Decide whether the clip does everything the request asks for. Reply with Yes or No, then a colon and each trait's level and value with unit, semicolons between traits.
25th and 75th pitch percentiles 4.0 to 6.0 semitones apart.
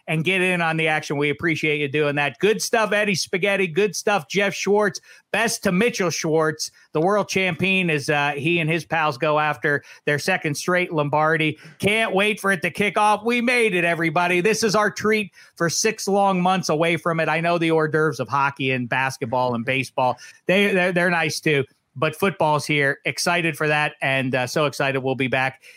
Yes: average, 4.7 semitones